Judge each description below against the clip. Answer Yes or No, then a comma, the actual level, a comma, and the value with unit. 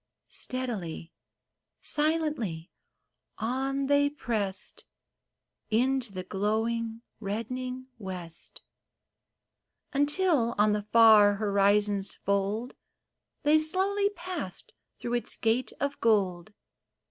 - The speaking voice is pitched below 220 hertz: No, high, 230 Hz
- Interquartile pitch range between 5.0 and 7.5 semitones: Yes, average, 5.3 semitones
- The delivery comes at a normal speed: No, slow, 85 wpm